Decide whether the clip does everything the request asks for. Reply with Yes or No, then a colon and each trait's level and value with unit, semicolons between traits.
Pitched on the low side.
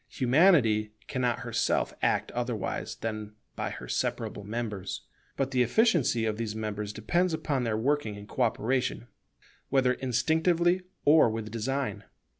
Yes: low, 120 Hz